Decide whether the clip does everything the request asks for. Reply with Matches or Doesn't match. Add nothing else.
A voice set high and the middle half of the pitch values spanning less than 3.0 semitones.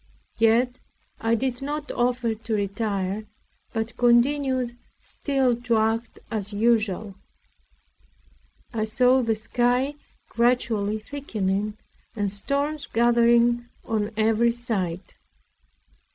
Matches